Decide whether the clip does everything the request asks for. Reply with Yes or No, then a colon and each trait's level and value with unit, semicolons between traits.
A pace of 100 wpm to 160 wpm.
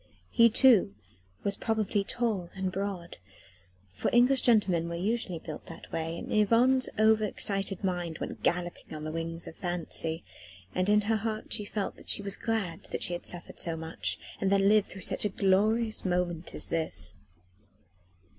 No: average, 175 wpm